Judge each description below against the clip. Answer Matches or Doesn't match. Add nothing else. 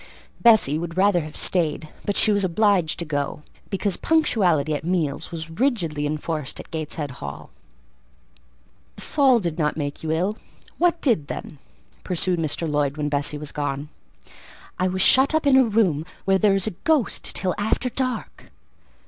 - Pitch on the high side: Doesn't match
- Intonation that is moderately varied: Doesn't match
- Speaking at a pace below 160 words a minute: Doesn't match